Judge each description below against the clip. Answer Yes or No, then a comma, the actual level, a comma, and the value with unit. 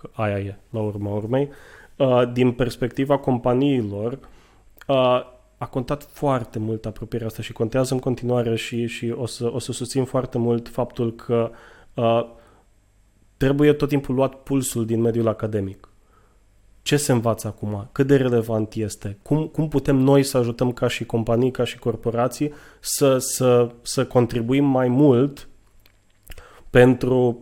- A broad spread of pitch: No, narrow, 2.6 semitones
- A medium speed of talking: Yes, average, 140 wpm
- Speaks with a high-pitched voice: No, low, 120 Hz